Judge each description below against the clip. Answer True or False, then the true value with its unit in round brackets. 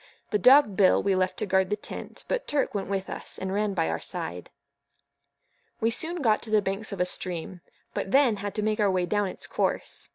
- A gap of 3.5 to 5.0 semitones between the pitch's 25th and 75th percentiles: False (2.4 semitones)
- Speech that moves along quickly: True (225 wpm)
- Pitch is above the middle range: True (205 Hz)